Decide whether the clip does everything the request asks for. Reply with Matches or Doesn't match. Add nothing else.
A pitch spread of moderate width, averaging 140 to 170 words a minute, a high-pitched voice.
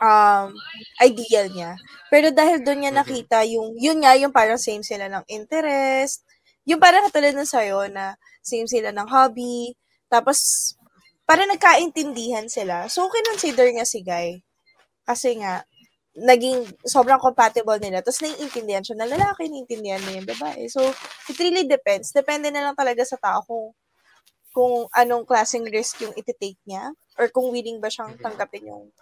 Matches